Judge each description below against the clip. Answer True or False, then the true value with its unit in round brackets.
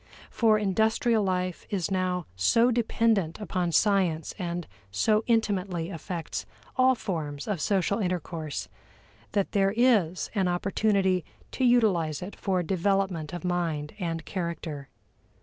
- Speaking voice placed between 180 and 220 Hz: True (185 Hz)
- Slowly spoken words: True (125 wpm)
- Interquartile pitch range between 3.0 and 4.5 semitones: True (3.7 semitones)